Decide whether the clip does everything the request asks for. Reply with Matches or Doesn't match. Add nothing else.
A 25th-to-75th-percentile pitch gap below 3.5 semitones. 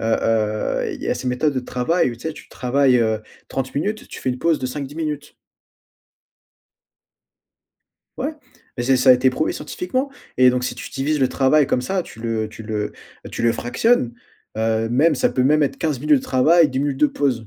Doesn't match